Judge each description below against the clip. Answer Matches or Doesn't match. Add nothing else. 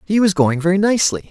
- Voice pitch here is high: Doesn't match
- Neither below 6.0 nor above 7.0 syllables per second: Matches